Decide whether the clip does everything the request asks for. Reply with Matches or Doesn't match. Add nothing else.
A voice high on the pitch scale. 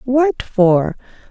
Matches